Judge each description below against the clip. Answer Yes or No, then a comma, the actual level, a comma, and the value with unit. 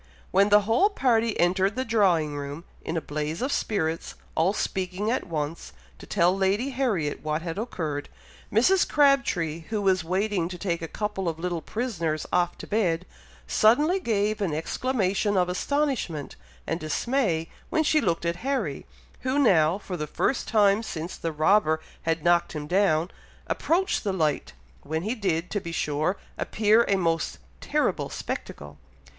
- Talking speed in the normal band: Yes, average, 160 wpm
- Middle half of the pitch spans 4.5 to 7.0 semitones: Yes, average, 5.2 semitones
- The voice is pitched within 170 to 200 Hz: Yes, medium, 185 Hz